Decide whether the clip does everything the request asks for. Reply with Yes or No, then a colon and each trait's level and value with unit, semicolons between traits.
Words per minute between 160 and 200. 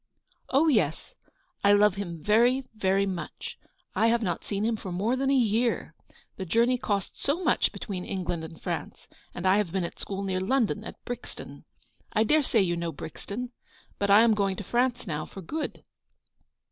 Yes: average, 190 wpm